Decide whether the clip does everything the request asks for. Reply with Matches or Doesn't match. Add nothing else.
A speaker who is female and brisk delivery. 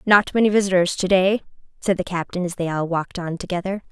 Matches